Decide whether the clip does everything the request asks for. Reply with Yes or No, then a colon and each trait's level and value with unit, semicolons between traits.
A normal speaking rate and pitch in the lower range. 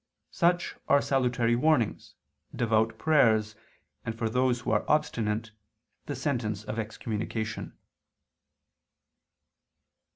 No: slow, 95 wpm; low, 115 Hz